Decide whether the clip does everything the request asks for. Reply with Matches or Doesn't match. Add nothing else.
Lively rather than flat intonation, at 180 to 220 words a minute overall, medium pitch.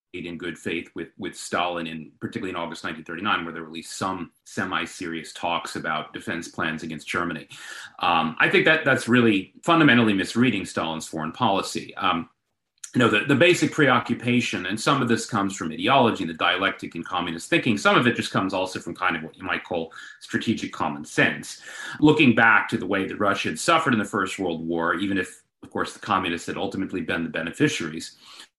Doesn't match